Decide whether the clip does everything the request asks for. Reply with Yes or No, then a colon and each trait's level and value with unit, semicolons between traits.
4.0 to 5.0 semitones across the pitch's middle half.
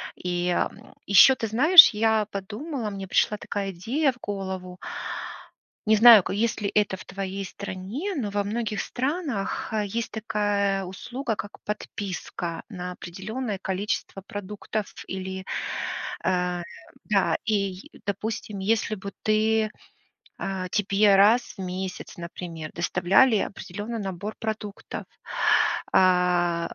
No: average, 2.7 semitones